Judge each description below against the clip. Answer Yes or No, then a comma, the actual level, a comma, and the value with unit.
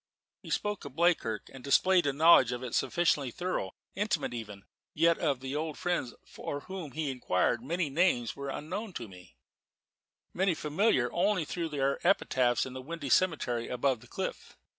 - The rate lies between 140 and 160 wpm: No, average, 170 wpm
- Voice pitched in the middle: Yes, medium, 145 Hz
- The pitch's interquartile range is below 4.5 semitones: No, wide, 5.6 semitones